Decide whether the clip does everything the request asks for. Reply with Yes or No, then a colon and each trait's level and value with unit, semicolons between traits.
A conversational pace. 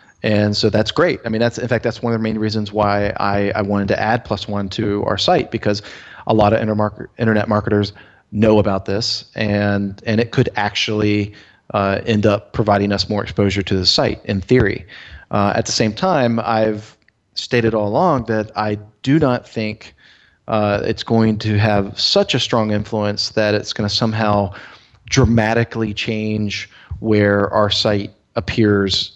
Yes: average, 180 wpm